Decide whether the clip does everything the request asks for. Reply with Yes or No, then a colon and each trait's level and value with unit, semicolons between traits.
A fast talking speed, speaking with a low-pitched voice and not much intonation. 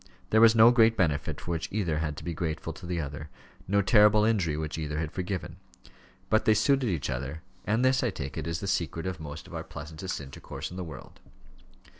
No: fast, 220 wpm; very low, 85 Hz; wide, 5.4 semitones